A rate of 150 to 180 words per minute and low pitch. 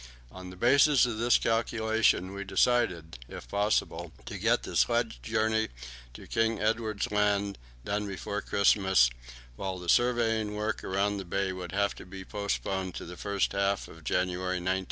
Yes: average, 165 wpm; low, 100 Hz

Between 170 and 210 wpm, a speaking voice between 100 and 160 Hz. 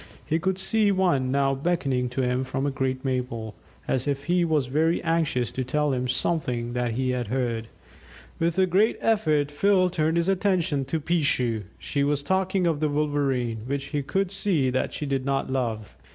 Yes: average, 190 wpm; medium, 140 Hz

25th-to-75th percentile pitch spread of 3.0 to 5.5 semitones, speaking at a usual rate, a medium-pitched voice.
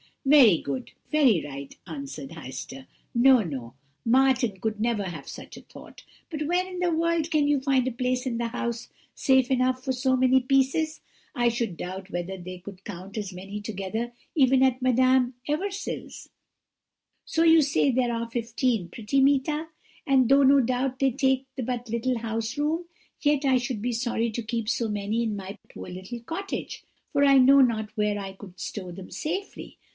No: average, 4.5 semitones; average, 180 wpm; high, 245 Hz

